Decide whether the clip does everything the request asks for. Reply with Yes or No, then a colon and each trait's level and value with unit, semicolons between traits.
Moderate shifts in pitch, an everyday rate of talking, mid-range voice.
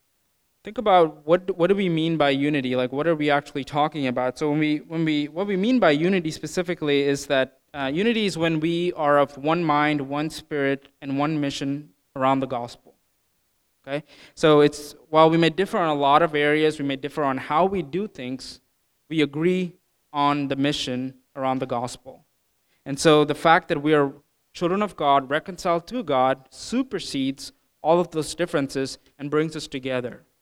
Yes: average, 3.2 semitones; average, 190 wpm; medium, 150 Hz